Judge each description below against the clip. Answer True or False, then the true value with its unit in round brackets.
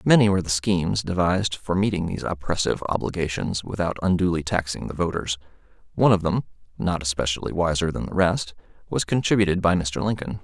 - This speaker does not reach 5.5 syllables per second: False (6.2 syllables/s)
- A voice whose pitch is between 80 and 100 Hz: True (90 Hz)